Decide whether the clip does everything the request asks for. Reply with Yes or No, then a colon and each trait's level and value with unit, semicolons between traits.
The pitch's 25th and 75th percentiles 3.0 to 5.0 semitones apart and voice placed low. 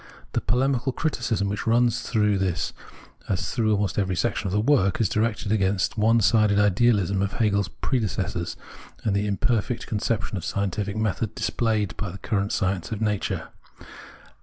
No: narrow, 2.5 semitones; low, 105 Hz